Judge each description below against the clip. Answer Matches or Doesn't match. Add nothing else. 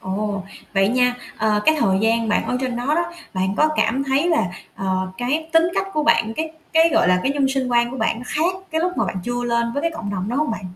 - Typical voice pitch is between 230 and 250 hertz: Matches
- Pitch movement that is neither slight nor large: Doesn't match